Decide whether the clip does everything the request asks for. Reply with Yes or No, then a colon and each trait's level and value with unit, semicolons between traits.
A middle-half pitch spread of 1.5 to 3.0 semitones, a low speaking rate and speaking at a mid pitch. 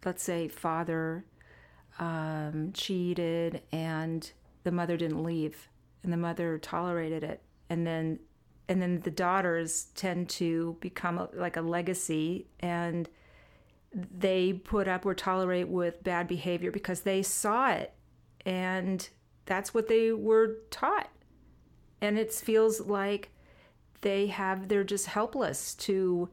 Yes: narrow, 2.6 semitones; slow, 130 wpm; medium, 175 Hz